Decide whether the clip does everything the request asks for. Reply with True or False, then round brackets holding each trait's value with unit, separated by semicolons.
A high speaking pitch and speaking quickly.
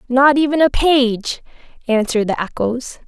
False (255 Hz; 135 wpm)